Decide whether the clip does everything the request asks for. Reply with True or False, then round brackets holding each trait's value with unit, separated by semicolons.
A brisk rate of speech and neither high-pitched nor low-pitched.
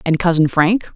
False (190 wpm; 175 Hz)